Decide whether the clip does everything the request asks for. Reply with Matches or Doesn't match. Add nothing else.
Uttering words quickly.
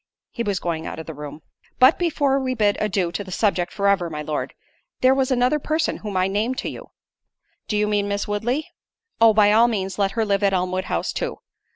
Matches